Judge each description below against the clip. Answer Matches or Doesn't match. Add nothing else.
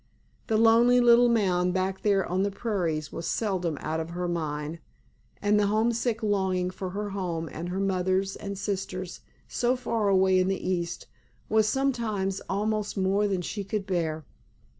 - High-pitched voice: Matches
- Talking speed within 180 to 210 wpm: Doesn't match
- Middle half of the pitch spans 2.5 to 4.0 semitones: Matches